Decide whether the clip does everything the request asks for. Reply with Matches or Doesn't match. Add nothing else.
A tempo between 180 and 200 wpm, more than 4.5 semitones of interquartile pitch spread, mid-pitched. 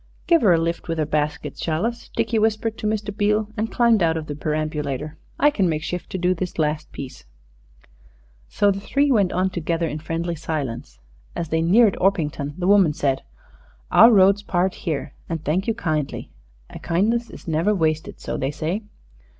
Matches